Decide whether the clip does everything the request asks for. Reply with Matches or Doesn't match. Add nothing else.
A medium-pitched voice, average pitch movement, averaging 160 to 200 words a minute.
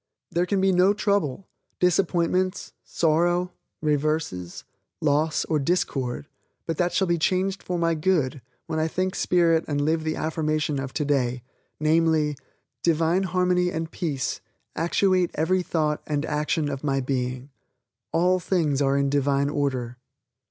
Doesn't match